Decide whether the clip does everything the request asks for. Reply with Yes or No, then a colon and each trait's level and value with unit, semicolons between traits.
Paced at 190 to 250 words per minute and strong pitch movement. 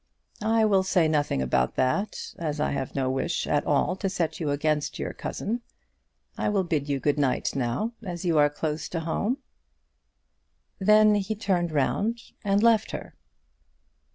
No: average, 165 wpm; wide, 5.9 semitones